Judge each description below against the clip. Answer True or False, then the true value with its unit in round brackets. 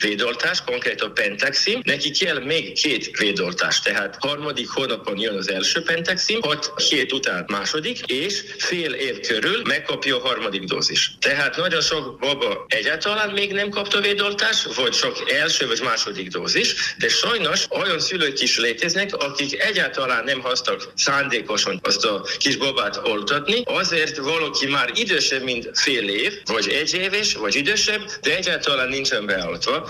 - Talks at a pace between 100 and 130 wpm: False (150 wpm)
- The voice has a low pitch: False (205 Hz)